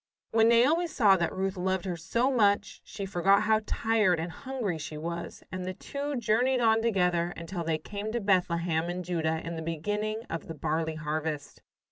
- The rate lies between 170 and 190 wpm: Yes, average, 185 wpm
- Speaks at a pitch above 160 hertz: Yes, medium, 185 Hz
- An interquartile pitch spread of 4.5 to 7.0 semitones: Yes, average, 5.0 semitones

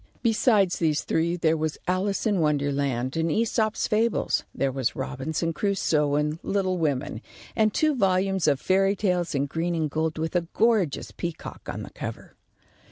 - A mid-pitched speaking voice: Yes, medium, 165 Hz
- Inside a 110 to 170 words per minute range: Yes, average, 165 wpm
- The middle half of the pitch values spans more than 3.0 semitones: Yes, average, 4.7 semitones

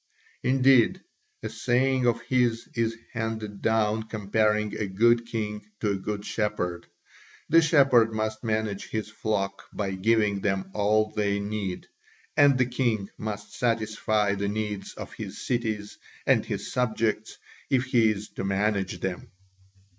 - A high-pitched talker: No, low, 110 Hz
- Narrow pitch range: Yes, narrow, 2.2 semitones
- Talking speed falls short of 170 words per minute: Yes, average, 140 wpm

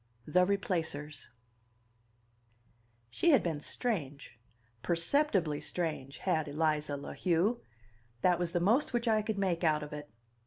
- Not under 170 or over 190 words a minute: No, average, 140 wpm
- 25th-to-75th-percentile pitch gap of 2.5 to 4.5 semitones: No, average, 5.0 semitones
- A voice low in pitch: No, medium, 170 Hz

